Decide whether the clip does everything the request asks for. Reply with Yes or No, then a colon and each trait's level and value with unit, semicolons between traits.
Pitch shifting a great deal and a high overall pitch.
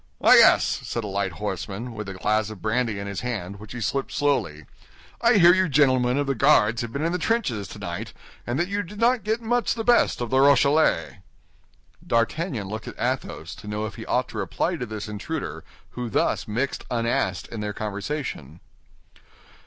No: wide, 5.9 semitones; low, 120 Hz